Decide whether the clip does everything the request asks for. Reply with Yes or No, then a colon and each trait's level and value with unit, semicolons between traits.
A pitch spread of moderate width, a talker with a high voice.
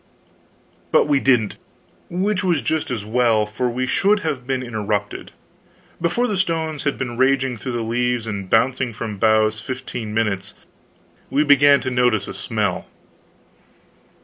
No: average, 4.4 semitones; low, 125 Hz